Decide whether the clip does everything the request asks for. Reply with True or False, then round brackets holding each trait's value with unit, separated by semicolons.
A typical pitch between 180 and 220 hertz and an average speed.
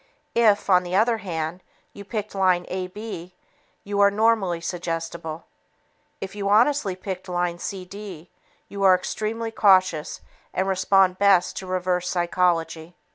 False (185 Hz; 130 wpm)